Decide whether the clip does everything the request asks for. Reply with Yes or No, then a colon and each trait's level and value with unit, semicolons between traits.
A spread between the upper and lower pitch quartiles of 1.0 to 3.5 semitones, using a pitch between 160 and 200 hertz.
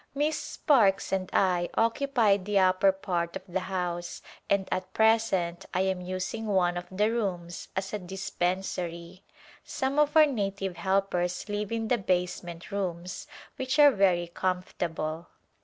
Yes: average, 2.9 semitones; high, 190 Hz